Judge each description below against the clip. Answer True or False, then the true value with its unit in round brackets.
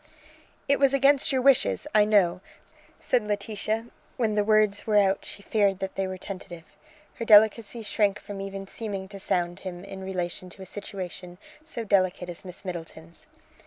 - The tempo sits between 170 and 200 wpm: True (175 wpm)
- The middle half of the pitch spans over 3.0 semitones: False (2.5 semitones)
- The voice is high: True (200 Hz)